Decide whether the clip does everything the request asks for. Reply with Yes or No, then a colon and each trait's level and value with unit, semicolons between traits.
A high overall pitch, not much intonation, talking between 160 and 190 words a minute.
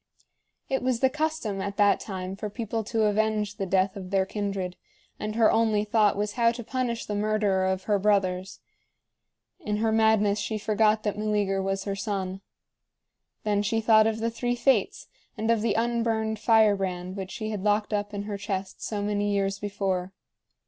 Yes: high, 210 Hz; narrow, 2.0 semitones; average, 185 wpm